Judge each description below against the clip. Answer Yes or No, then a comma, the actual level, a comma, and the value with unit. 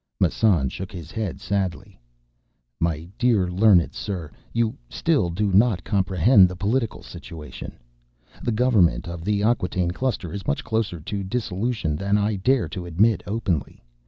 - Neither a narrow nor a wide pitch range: Yes, average, 4.0 semitones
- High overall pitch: No, low, 100 Hz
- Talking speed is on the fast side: No, average, 145 wpm